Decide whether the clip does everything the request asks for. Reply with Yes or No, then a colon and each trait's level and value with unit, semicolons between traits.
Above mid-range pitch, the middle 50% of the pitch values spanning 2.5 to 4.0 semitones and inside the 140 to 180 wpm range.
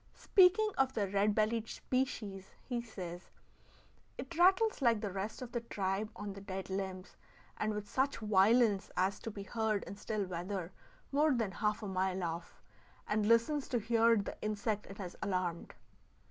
Yes: high, 210 Hz; average, 3.3 semitones; average, 170 wpm